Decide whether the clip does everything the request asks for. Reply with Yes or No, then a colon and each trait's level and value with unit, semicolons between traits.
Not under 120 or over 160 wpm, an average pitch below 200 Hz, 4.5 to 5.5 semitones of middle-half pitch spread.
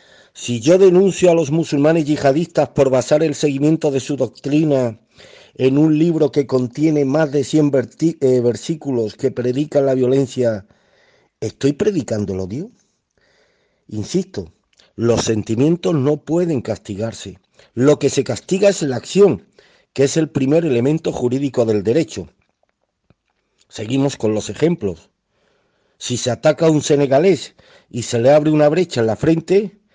Yes: average, 140 wpm; medium, 140 Hz; average, 4.8 semitones